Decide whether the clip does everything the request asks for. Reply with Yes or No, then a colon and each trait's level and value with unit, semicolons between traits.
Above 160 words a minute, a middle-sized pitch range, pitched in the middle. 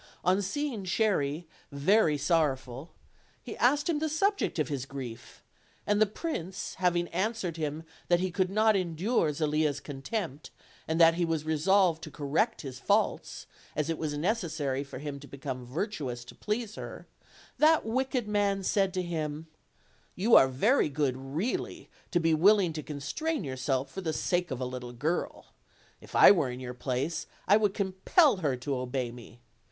No: average, 170 wpm; wide, 6.4 semitones; medium, 165 Hz